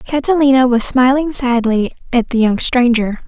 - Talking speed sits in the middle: Yes, average, 145 wpm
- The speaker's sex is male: No, female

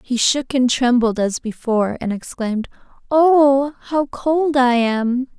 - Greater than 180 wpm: No, average, 145 wpm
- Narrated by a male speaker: No, female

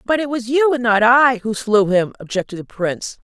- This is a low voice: No, high, 230 Hz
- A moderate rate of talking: No, fast, 235 wpm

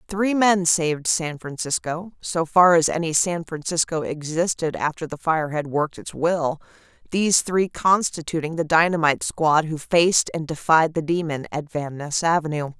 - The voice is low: No, medium, 165 Hz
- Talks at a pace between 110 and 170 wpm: Yes, average, 165 wpm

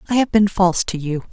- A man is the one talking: No, female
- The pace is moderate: No, fast, 275 wpm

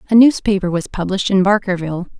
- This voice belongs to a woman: Yes, female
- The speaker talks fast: No, average, 165 wpm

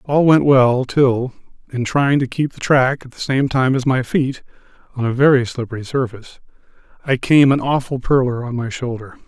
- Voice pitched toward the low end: Yes, low, 130 Hz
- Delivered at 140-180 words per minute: No, average, 195 wpm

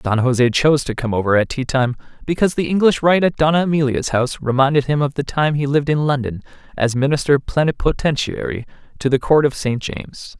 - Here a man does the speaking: Yes, male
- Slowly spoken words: No, average, 200 wpm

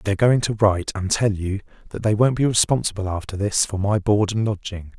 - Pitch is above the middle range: No, low, 105 Hz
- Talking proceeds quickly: Yes, fast, 230 wpm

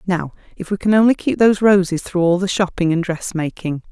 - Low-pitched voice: No, medium, 185 Hz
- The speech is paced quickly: Yes, fast, 215 wpm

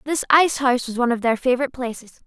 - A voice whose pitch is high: Yes, very high, 255 Hz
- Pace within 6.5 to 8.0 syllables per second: Yes, 7.7 syllables/s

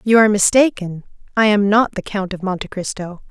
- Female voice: Yes, female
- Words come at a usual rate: Yes, average, 180 wpm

